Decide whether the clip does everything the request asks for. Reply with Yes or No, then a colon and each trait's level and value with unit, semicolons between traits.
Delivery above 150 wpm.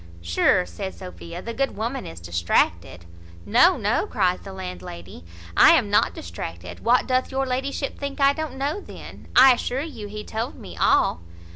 Yes: average, 170 wpm